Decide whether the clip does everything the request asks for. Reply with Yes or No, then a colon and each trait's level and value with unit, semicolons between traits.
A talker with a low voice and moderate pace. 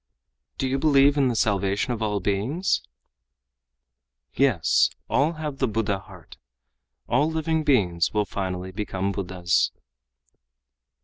No: low, 110 Hz; slow, 120 wpm